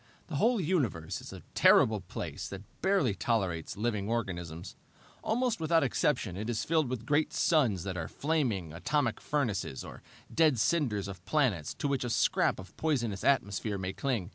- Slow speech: No, average, 165 wpm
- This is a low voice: Yes, low, 115 Hz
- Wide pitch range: Yes, wide, 7.6 semitones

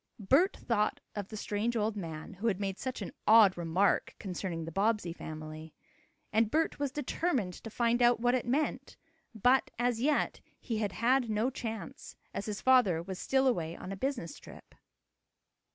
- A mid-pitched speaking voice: No, high, 215 Hz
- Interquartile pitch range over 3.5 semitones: Yes, average, 4.7 semitones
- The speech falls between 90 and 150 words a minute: No, average, 175 wpm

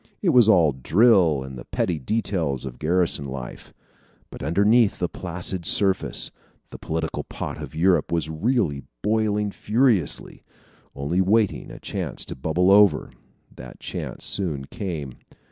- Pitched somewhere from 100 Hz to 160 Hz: No, very low, 90 Hz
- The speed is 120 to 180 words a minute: Yes, average, 140 wpm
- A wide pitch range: Yes, wide, 6.0 semitones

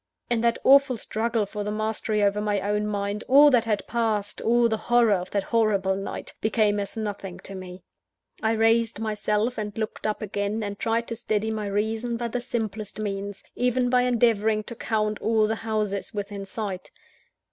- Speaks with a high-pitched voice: Yes, high, 215 Hz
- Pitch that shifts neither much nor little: No, narrow, 2.0 semitones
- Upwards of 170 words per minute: Yes, average, 185 wpm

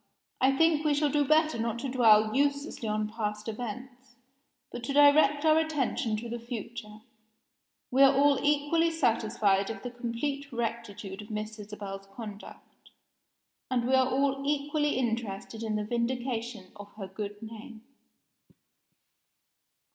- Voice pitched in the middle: No, high, 235 Hz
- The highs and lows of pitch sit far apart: No, average, 4.7 semitones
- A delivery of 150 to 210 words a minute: No, average, 140 wpm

